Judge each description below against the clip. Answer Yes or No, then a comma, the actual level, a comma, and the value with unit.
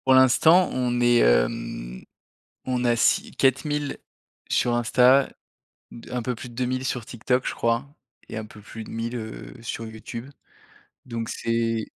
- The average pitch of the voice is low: Yes, low, 120 Hz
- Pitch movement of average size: No, narrow, 2.1 semitones